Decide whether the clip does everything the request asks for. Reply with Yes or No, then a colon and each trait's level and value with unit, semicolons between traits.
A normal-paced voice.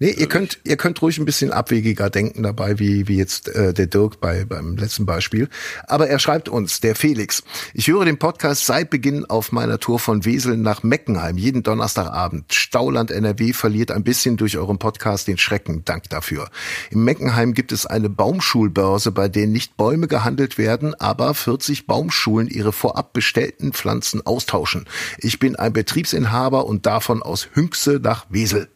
Yes: average, 175 wpm